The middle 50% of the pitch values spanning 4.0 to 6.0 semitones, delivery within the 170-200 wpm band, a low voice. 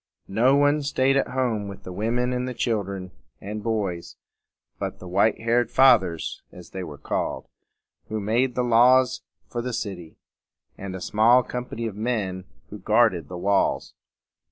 No: average, 4.4 semitones; average, 155 wpm; low, 110 Hz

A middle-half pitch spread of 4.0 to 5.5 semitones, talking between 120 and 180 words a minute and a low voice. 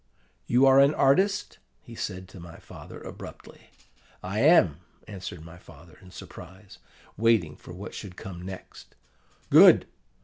Yes: average, 5.1 semitones; average, 140 wpm; very low, 95 Hz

